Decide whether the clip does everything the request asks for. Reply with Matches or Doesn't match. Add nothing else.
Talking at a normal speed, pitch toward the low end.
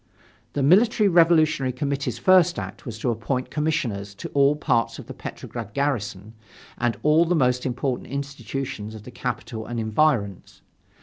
Matches